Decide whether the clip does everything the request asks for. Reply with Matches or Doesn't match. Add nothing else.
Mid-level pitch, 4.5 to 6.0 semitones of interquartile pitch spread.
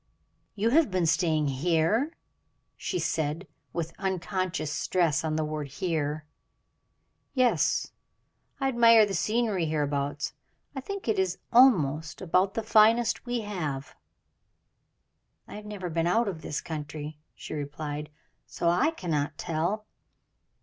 Matches